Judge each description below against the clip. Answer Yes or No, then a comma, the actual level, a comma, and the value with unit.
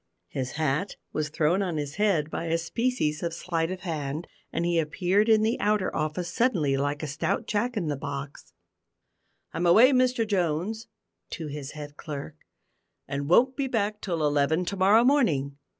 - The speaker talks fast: No, average, 175 wpm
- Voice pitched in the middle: Yes, medium, 170 Hz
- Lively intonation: Yes, wide, 5.8 semitones